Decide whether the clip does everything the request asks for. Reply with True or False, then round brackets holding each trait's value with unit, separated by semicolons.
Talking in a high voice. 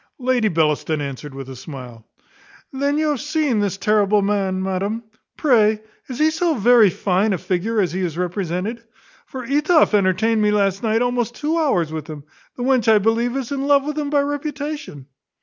True (220 Hz)